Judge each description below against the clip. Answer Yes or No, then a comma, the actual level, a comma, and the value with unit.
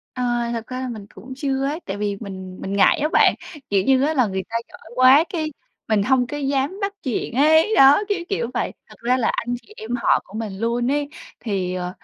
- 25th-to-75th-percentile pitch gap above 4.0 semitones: Yes, average, 5.1 semitones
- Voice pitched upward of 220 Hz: Yes, high, 245 Hz